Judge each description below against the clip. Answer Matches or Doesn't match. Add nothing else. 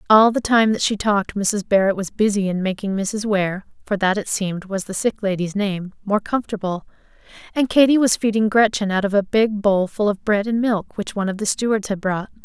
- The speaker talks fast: Matches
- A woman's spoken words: Matches